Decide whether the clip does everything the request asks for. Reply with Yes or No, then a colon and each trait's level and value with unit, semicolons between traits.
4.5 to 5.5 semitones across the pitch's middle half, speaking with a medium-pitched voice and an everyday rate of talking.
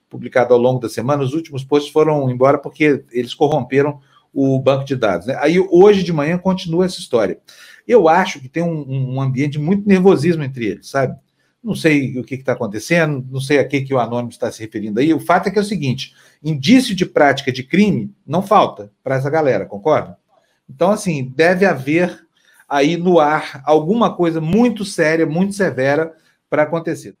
No: average, 4.8 semitones; medium, 150 Hz; fast, 195 wpm